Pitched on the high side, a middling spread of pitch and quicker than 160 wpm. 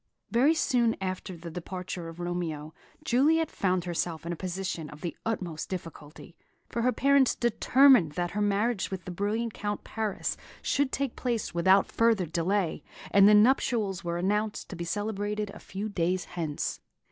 Yes: high, 195 Hz; average, 4.6 semitones; average, 170 wpm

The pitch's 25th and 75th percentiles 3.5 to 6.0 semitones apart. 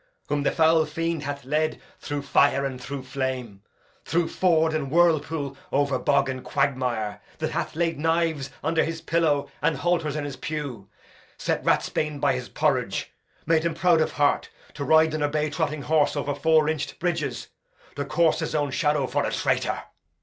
No: narrow, 2.4 semitones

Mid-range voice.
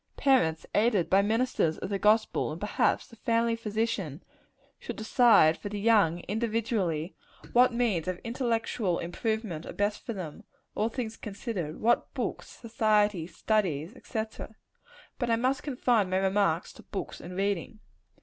No: high, 210 Hz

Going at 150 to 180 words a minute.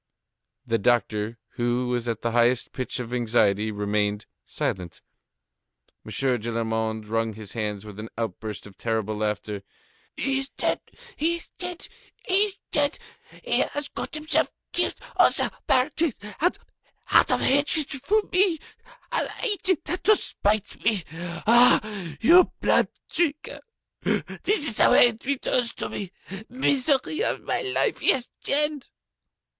No: average, 140 wpm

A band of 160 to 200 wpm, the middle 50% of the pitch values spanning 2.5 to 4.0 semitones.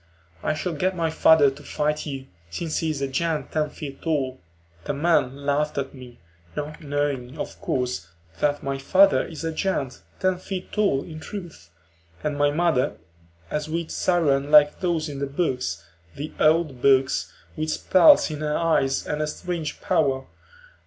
Yes: average, 170 wpm; average, 3.1 semitones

